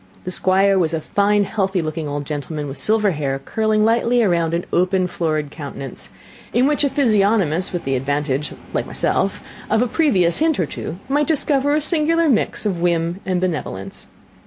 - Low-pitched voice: No, medium, 185 Hz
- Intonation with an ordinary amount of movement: No, wide, 6.3 semitones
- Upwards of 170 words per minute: Yes, average, 180 wpm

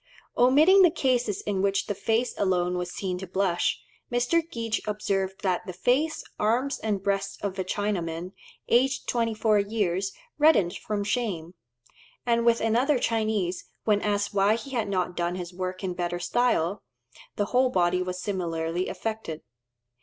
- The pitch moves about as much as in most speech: Yes, average, 4.1 semitones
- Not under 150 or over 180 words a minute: Yes, average, 155 wpm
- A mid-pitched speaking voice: No, high, 205 Hz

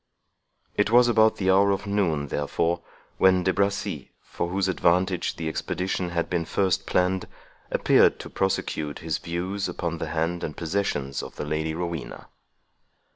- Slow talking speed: No, average, 155 wpm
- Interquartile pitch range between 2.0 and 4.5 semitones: Yes, average, 2.7 semitones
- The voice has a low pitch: Yes, very low, 90 Hz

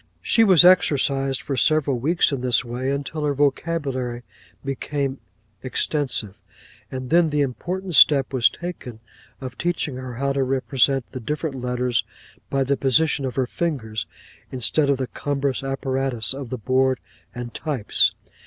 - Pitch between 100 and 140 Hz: Yes, low, 135 Hz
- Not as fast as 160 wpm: Yes, average, 150 wpm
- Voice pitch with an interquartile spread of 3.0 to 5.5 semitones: No, narrow, 2.4 semitones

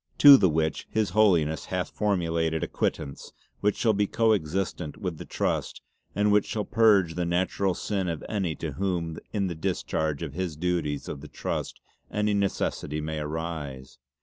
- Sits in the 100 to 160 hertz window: No, very low, 90 Hz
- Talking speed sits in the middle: Yes, average, 175 wpm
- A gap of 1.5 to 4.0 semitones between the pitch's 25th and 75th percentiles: No, average, 4.4 semitones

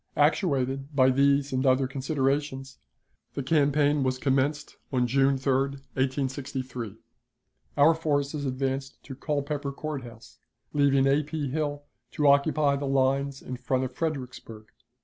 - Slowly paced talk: Yes, slow, 130 wpm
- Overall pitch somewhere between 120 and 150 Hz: Yes, medium, 140 Hz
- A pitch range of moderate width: No, narrow, 1.6 semitones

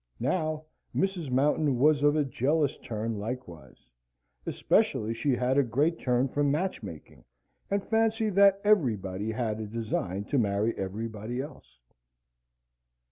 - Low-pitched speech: Yes, low, 130 Hz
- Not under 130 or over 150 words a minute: Yes, slow, 135 wpm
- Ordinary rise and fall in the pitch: No, wide, 6.0 semitones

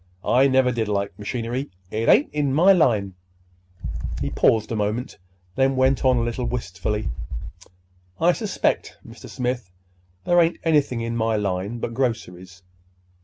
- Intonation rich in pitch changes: No, average, 4.0 semitones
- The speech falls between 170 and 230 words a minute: No, average, 145 wpm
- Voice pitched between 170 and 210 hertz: No, low, 120 Hz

